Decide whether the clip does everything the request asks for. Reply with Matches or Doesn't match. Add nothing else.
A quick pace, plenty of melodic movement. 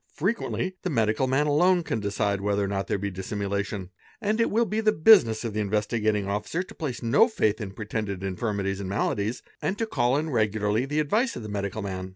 Matches